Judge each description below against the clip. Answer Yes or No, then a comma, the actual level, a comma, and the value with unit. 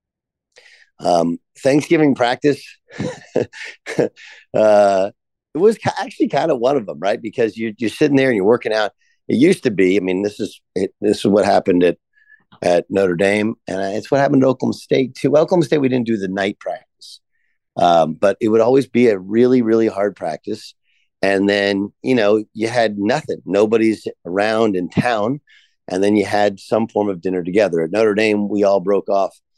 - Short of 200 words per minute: Yes, average, 190 wpm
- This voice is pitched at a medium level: No, low, 110 Hz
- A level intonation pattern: No, average, 4.3 semitones